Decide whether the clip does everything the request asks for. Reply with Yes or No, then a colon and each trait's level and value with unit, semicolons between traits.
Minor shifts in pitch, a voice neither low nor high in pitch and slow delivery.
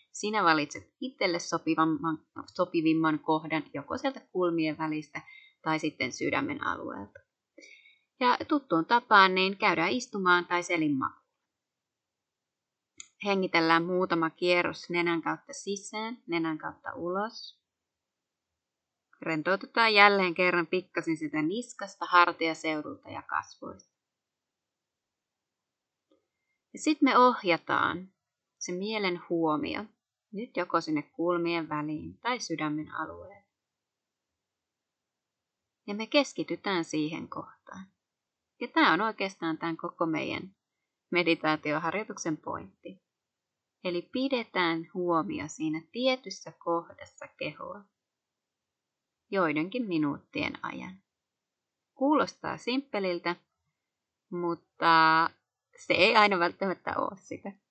No: average, 4.3 semitones; medium, 175 Hz; slow, 90 wpm